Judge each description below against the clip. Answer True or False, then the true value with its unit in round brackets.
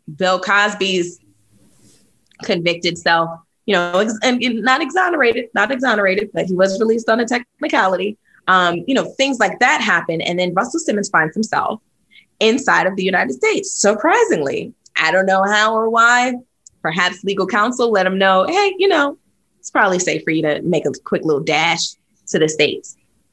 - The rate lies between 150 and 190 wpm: True (175 wpm)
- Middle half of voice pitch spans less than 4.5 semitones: False (5.4 semitones)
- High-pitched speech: True (205 Hz)